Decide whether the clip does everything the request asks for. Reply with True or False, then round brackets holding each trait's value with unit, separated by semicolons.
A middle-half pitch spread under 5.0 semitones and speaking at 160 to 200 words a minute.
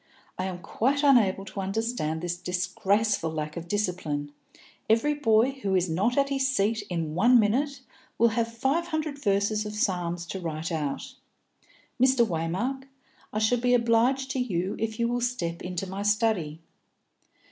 False (5.6 semitones; 165 wpm)